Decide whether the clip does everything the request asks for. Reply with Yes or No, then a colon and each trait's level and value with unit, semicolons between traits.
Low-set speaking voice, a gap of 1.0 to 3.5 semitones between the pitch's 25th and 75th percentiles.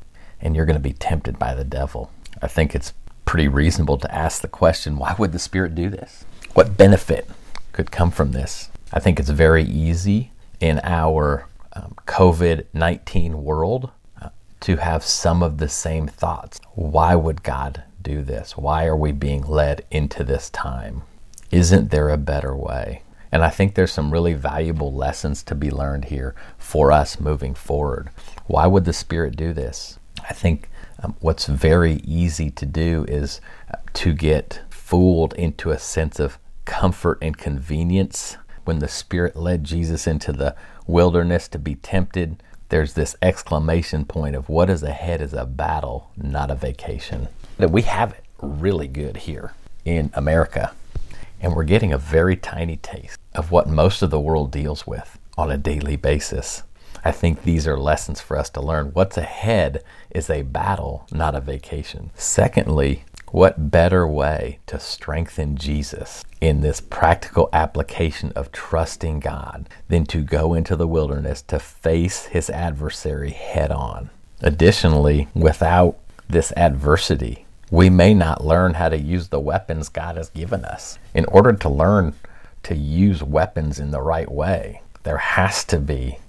Yes: very low, 80 Hz; average, 3.0 semitones